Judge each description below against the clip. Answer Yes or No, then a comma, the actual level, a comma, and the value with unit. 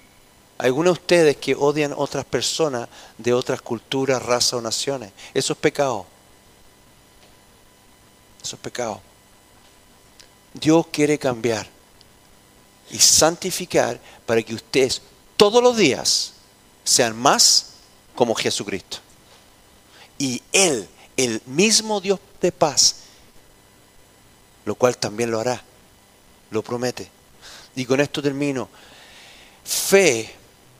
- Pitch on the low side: Yes, low, 125 Hz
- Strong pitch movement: Yes, wide, 5.9 semitones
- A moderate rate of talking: No, slow, 105 wpm